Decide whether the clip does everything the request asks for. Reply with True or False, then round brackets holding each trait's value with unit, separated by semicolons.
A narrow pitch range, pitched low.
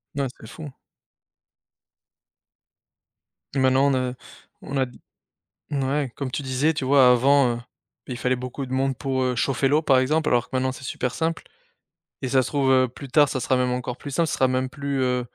True (1.7 semitones; 130 Hz)